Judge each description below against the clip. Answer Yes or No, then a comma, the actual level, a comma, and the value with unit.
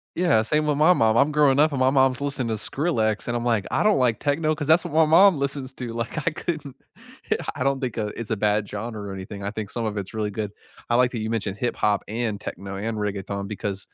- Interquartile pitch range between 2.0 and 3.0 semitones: No, average, 5.2 semitones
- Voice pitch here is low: Yes, low, 120 Hz